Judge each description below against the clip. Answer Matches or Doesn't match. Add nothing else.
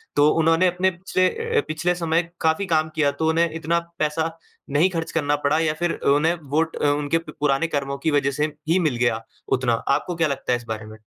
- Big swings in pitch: Doesn't match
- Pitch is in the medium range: Matches